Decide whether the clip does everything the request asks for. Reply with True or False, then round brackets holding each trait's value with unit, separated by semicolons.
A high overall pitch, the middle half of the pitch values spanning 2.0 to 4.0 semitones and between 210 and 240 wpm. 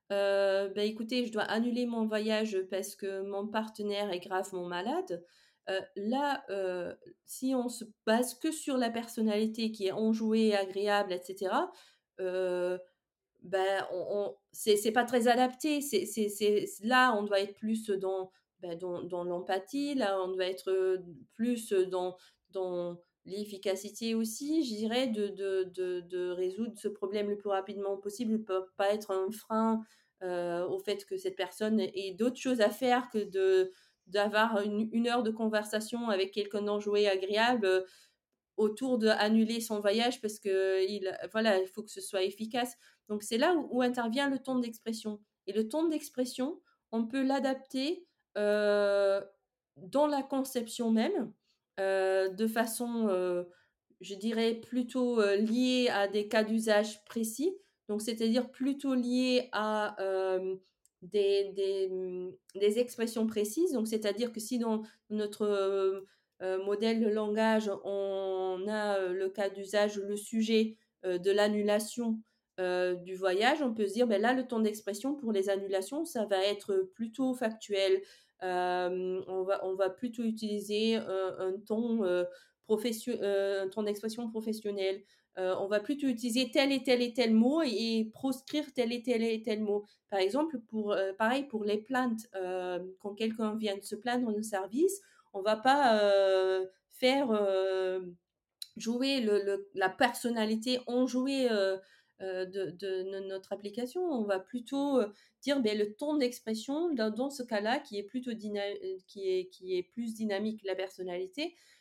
False (210 Hz; 3.6 semitones; 160 wpm)